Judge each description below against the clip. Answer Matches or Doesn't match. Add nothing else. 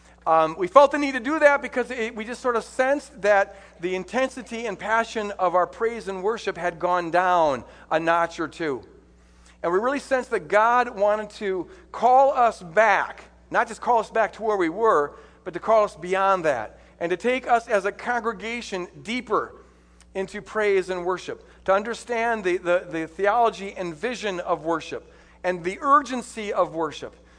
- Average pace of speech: Matches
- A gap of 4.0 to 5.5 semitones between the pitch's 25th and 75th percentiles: Matches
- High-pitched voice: Matches